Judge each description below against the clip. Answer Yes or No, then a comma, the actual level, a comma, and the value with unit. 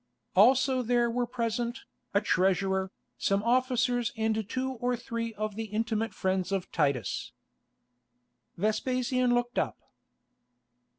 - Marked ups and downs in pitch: No, average, 3.7 semitones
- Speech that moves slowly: Yes, slow, 115 wpm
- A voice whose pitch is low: No, high, 230 Hz